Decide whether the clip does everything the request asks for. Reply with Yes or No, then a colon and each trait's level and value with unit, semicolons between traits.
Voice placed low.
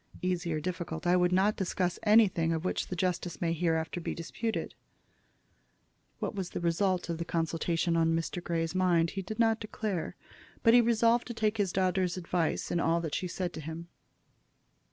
No: medium, 175 Hz